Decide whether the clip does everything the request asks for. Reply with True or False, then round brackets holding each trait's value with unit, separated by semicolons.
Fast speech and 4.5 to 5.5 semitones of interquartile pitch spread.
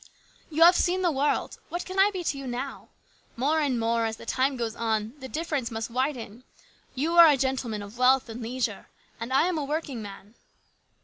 True (210 wpm; 4.9 semitones)